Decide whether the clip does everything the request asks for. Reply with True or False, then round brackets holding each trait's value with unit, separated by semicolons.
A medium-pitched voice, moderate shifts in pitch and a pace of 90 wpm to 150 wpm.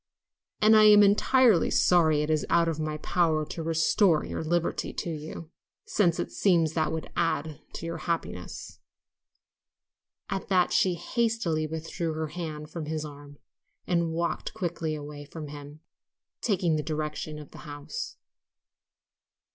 False (160 Hz; 2.3 semitones; 145 wpm)